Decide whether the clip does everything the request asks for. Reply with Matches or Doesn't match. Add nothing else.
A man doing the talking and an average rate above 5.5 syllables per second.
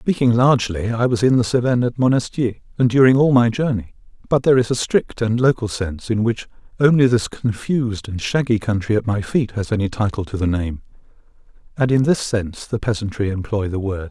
Matches